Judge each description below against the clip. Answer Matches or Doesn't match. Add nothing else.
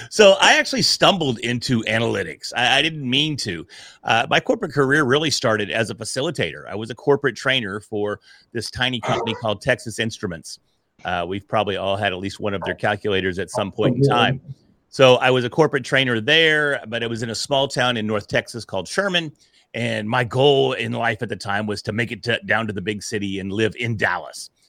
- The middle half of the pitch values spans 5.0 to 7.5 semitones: Doesn't match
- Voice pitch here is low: Matches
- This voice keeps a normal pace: Doesn't match